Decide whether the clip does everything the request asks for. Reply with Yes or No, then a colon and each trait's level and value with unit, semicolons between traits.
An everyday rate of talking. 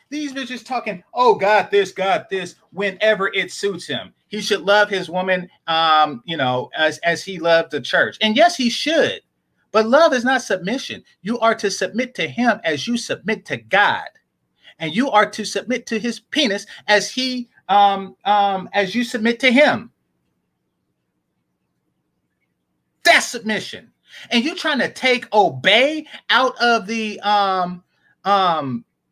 Yes: average, 155 wpm